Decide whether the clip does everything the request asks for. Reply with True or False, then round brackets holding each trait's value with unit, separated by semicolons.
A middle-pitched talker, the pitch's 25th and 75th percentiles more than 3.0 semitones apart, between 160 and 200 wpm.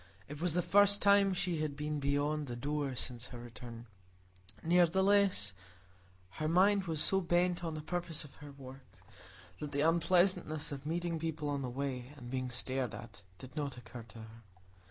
True (150 Hz; 5.2 semitones; 175 wpm)